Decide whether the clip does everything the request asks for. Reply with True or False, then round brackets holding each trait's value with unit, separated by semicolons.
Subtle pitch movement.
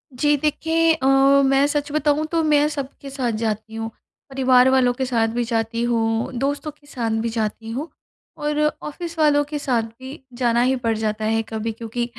False (4.4 semitones)